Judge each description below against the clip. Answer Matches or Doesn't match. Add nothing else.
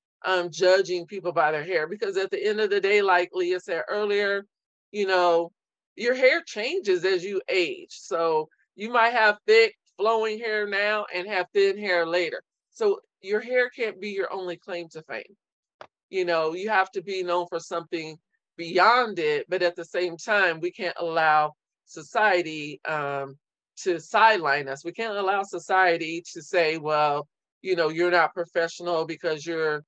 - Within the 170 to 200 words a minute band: Matches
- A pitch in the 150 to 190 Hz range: Matches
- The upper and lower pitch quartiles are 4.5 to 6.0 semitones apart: Matches